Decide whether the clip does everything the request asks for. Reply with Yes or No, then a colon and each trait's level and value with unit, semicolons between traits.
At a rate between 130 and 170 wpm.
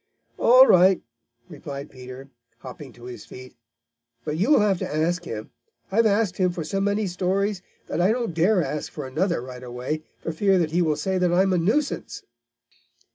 No: average, 185 wpm